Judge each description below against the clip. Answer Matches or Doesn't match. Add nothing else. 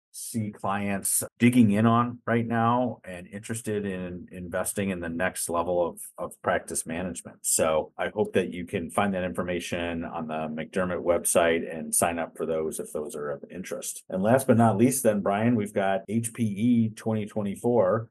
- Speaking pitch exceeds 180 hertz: Doesn't match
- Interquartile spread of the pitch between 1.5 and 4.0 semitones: Doesn't match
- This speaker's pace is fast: Doesn't match